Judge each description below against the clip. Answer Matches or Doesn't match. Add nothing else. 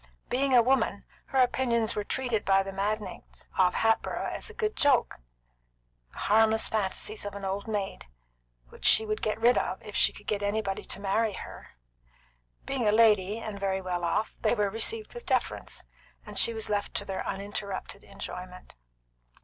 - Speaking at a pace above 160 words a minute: Matches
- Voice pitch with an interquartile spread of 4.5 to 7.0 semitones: Doesn't match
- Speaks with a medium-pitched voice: Doesn't match